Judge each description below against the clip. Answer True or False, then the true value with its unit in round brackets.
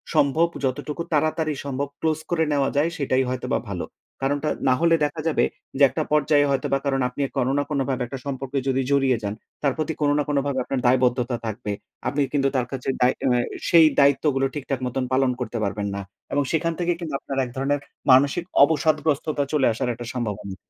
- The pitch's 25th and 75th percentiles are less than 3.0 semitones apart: True (2.5 semitones)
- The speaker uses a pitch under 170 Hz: True (140 Hz)